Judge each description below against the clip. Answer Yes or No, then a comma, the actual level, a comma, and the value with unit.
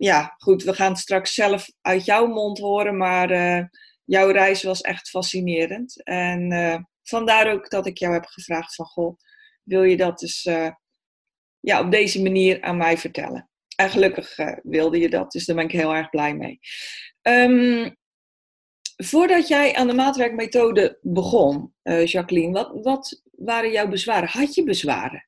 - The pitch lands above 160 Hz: Yes, high, 190 Hz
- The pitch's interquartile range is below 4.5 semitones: No, average, 4.9 semitones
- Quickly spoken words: No, average, 170 wpm